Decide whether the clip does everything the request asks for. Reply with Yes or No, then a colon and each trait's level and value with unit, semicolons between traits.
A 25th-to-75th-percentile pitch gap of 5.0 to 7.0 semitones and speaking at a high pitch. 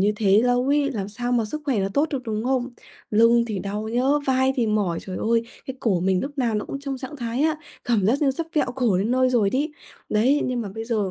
No: average, 3.9 semitones; high, 235 Hz